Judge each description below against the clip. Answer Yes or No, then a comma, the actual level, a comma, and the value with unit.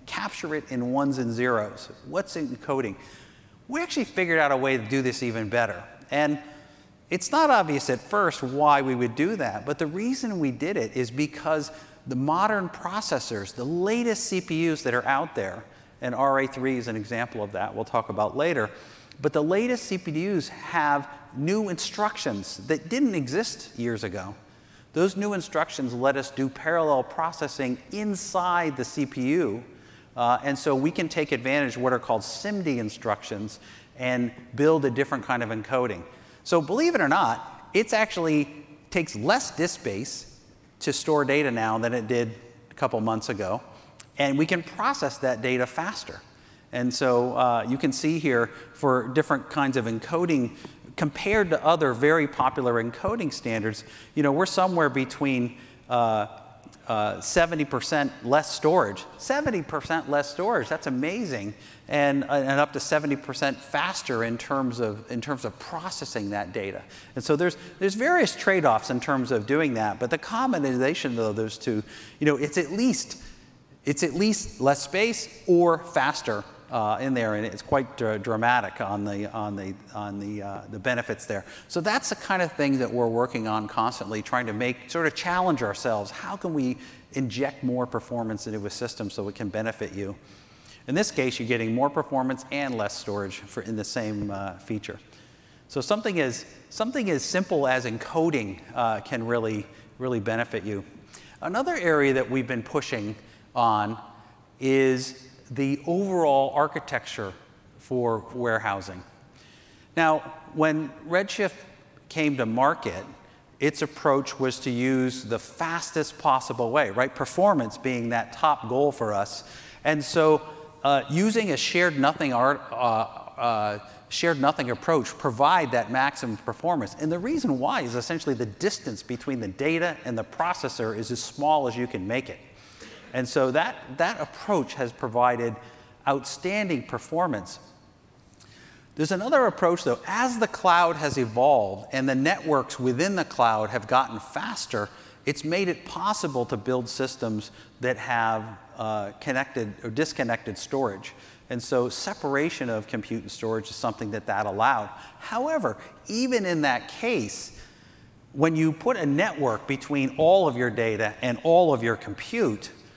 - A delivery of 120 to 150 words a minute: No, average, 160 wpm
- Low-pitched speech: Yes, low, 130 Hz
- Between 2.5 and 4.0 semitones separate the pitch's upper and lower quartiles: No, average, 5.3 semitones